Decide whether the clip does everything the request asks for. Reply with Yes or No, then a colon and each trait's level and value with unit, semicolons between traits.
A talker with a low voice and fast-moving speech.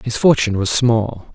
No: low, 115 Hz; average, 180 wpm